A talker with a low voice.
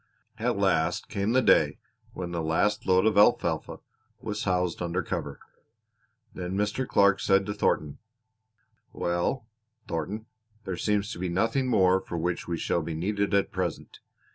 Yes: very low, 95 Hz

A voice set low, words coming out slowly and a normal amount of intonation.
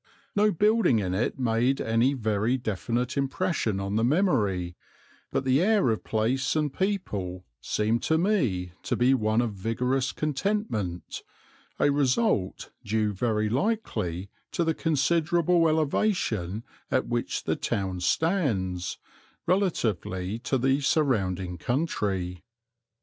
No: low, 120 Hz; slow, 120 wpm; wide, 7.7 semitones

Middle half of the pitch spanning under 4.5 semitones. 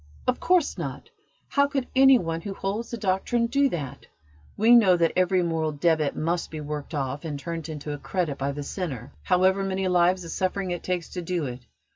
Yes: average, 4.1 semitones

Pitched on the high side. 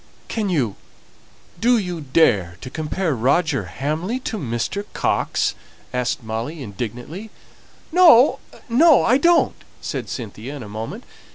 No: medium, 150 Hz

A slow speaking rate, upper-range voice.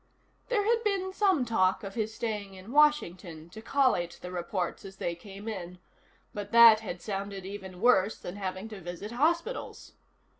No: average, 165 wpm; high, 205 Hz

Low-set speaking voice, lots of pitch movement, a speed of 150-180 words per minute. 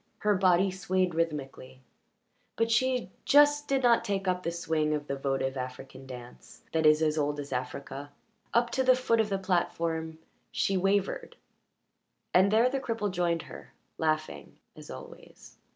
No: medium, 175 Hz; wide, 6.2 semitones; average, 160 wpm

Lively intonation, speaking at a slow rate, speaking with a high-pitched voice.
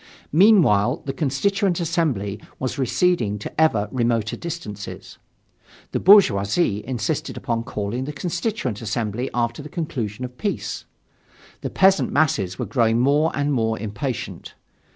No: wide, 6.7 semitones; slow, 130 wpm; low, 130 Hz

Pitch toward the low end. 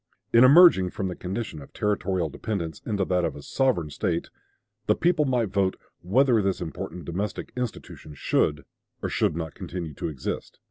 Yes: very low, 95 Hz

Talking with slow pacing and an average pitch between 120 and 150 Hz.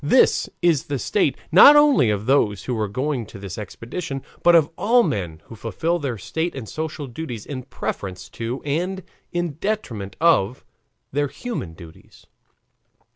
No: average, 160 wpm; low, 135 Hz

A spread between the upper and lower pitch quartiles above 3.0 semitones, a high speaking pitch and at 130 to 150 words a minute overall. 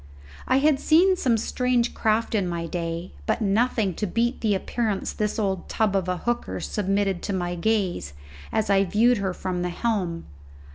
No: average, 4.3 semitones; high, 205 Hz; average, 180 wpm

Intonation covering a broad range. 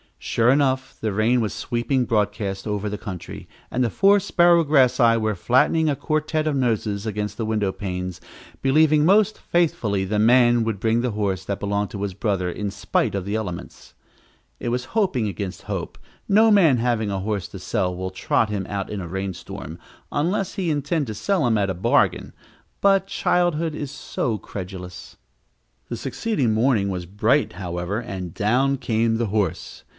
Yes: wide, 5.8 semitones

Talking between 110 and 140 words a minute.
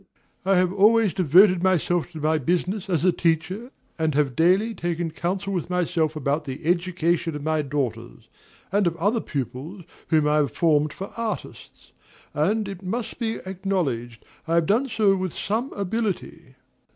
No: average, 165 wpm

